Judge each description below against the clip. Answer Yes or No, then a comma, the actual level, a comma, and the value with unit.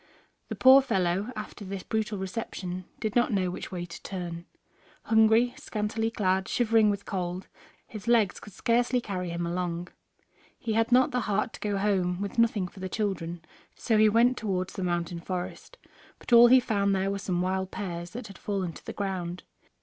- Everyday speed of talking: Yes, average, 190 wpm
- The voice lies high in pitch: Yes, high, 200 Hz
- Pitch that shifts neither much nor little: Yes, average, 3.6 semitones